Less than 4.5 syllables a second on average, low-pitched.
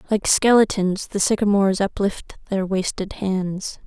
No: 4.3 syllables/s; high, 195 Hz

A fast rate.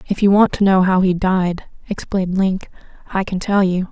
Yes: fast, 215 wpm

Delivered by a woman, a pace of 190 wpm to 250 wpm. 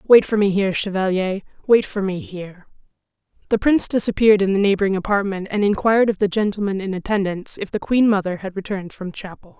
Yes: female; average, 195 wpm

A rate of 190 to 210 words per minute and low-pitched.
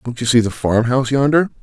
No: fast, 260 wpm; low, 125 Hz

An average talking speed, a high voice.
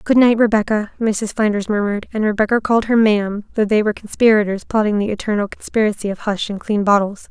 Yes: average, 195 wpm; high, 210 Hz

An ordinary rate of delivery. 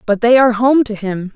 No: fast, 265 wpm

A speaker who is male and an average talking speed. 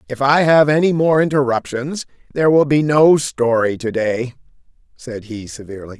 Yes: male; average, 160 wpm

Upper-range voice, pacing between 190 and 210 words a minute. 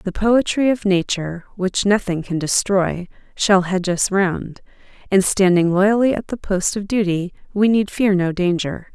No: high, 195 Hz; average, 170 wpm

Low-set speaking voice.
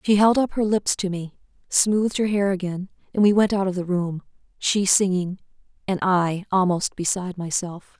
No: high, 190 Hz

